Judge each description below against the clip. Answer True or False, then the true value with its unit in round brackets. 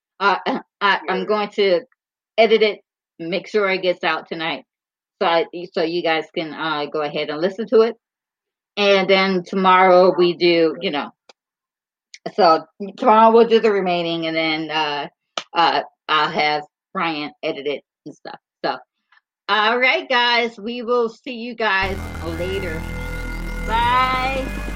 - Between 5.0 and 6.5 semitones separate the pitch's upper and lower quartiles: True (5.5 semitones)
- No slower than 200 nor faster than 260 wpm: False (150 wpm)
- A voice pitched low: False (190 Hz)